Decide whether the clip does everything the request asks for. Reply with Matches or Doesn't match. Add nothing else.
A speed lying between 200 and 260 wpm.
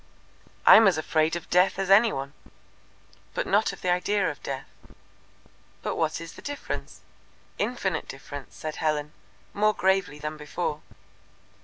Doesn't match